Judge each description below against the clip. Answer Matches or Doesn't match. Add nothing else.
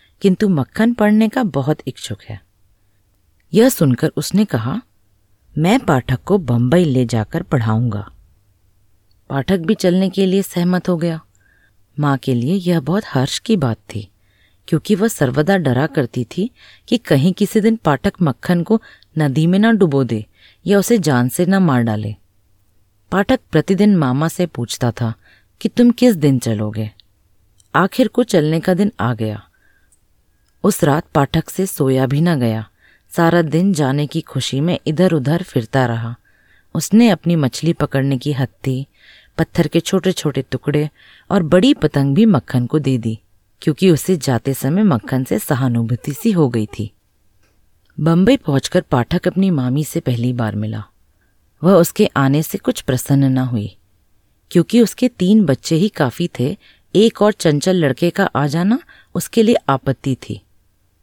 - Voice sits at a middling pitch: Matches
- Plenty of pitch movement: Matches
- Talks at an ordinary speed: Matches